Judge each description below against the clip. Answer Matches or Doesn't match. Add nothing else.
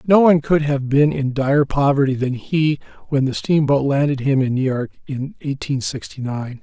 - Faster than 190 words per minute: Matches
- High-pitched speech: Doesn't match